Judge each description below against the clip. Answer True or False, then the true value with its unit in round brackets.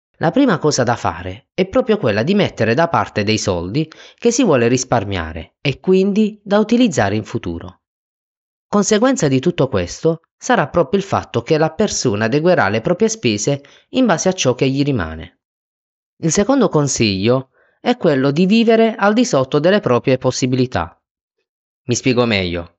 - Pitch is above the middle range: False (140 Hz)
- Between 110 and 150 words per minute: False (165 wpm)